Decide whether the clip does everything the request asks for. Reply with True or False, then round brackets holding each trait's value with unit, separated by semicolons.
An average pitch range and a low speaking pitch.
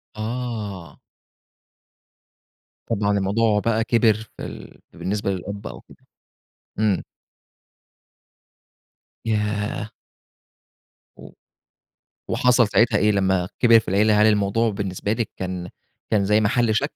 False (2.2 semitones; 105 Hz)